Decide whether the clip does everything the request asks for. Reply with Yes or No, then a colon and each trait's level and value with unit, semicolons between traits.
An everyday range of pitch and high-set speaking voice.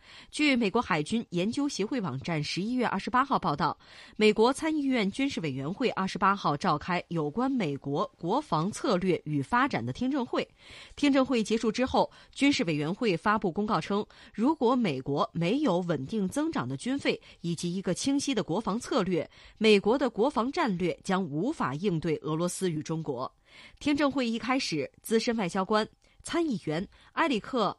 No: wide, 6.9 semitones; high, 210 Hz